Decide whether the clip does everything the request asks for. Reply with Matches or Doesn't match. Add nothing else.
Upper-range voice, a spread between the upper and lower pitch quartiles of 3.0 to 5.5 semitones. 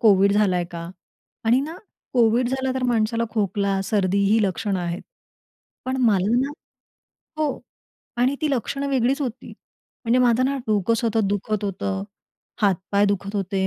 Matches